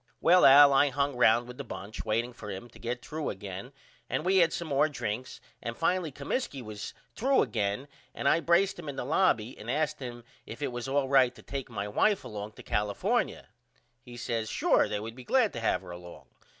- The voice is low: Yes, low, 125 Hz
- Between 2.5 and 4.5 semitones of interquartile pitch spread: No, average, 4.9 semitones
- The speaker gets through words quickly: Yes, fast, 215 wpm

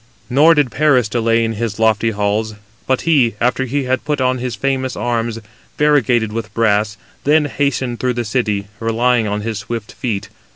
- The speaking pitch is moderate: No, low, 120 Hz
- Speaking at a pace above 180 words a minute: No, average, 175 wpm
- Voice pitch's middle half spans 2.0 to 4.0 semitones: Yes, average, 3.0 semitones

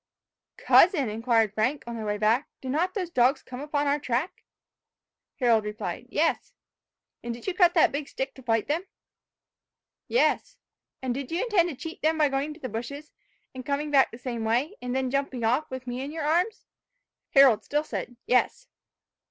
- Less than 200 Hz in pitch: No, very high, 270 Hz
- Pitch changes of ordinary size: Yes, average, 4.3 semitones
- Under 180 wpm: No, average, 185 wpm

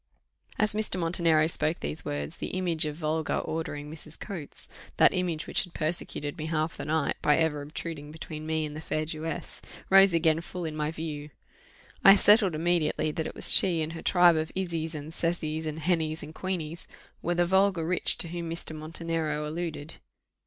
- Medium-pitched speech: Yes, medium, 160 Hz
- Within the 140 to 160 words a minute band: No, average, 190 wpm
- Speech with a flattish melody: Yes, narrow, 2.0 semitones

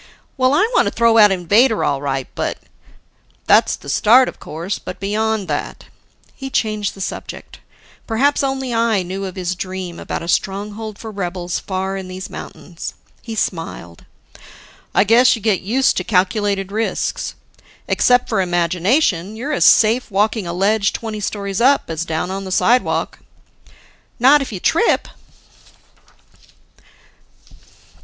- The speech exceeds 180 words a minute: No, average, 150 wpm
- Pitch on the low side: No, high, 205 Hz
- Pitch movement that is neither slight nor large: Yes, average, 3.7 semitones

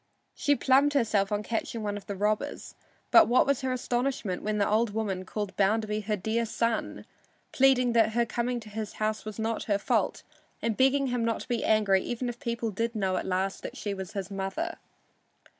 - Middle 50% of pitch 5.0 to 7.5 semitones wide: No, average, 2.8 semitones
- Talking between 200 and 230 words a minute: Yes, fast, 205 wpm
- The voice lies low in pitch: No, high, 220 Hz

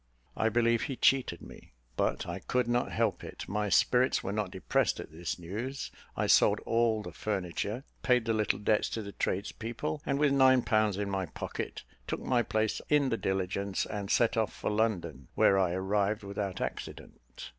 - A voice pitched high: No, low, 105 Hz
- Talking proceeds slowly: No, average, 185 wpm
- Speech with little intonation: No, average, 3.4 semitones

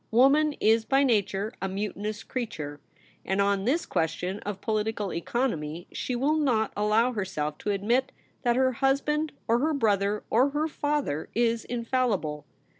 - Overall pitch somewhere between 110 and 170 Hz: No, high, 225 Hz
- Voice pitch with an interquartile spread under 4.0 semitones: No, average, 4.8 semitones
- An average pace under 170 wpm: Yes, average, 150 wpm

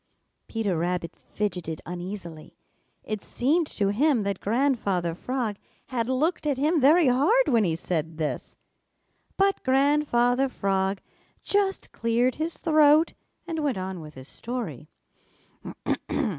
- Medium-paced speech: No, slow, 125 wpm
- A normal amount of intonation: No, wide, 7.7 semitones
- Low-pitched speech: No, high, 235 Hz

